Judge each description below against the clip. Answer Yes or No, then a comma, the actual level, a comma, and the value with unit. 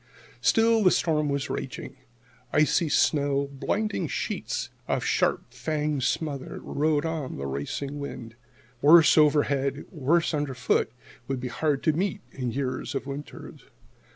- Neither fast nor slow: No, slow, 130 wpm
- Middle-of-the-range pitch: Yes, medium, 145 Hz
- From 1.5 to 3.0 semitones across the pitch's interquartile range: Yes, narrow, 2.6 semitones